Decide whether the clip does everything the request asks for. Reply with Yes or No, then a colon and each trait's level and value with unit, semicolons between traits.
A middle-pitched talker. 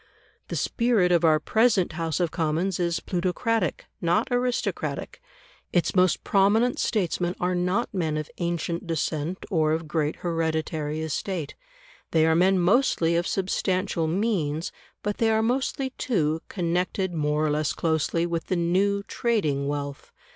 Yes: medium, 175 Hz